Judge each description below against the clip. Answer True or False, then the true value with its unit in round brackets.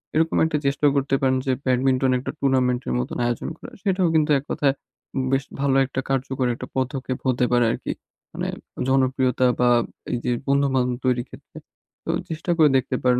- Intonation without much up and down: True (1.6 semitones)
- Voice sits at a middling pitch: False (130 Hz)